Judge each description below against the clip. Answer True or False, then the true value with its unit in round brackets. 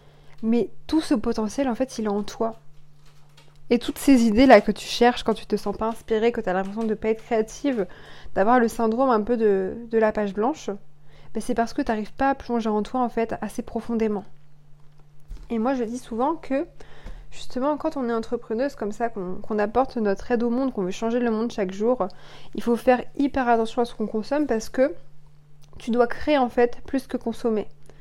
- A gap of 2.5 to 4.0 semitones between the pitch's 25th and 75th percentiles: True (3.2 semitones)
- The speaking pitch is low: False (230 Hz)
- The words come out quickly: True (225 wpm)